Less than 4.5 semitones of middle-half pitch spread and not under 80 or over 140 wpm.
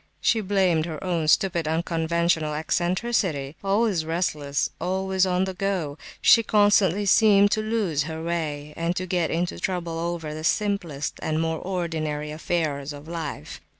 No: average, 3.4 semitones; average, 150 wpm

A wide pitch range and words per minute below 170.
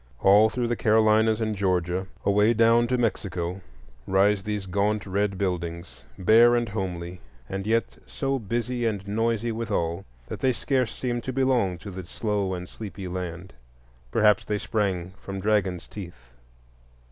No: average, 3.5 semitones; average, 150 wpm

